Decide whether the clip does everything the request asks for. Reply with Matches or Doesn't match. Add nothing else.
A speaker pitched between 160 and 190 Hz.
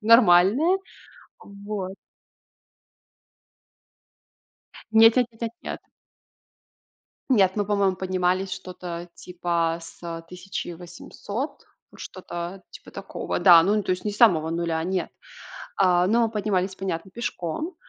Matches